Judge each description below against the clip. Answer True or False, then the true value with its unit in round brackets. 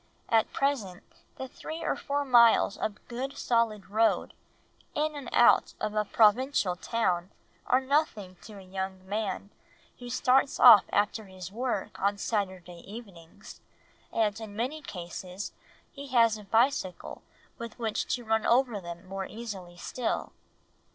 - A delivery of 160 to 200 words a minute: False (145 wpm)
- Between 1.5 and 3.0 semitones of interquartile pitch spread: False (4.2 semitones)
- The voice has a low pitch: False (215 Hz)